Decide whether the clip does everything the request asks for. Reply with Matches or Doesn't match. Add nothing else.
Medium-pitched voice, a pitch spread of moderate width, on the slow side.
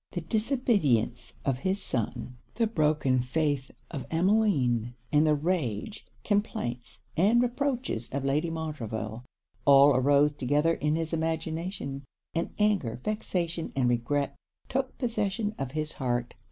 Doesn't match